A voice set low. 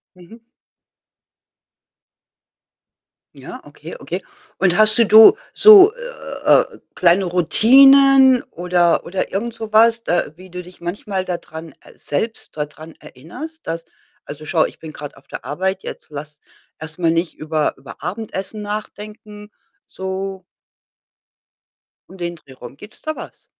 No: high, 190 Hz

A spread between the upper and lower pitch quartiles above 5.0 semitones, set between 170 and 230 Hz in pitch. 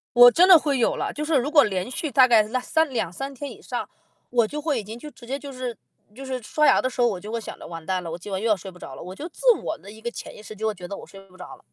No: wide, 5.6 semitones; high, 240 Hz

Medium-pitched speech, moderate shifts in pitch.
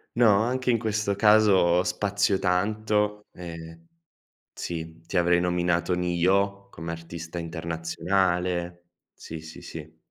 No: very low, 90 Hz; average, 3.3 semitones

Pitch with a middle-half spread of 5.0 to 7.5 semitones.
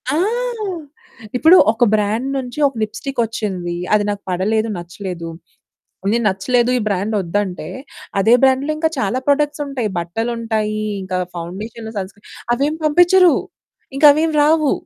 Yes: wide, 5.6 semitones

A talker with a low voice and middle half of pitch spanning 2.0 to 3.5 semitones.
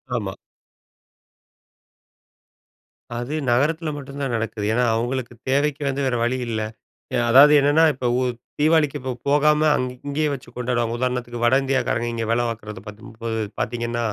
Yes: low, 125 Hz; average, 3.2 semitones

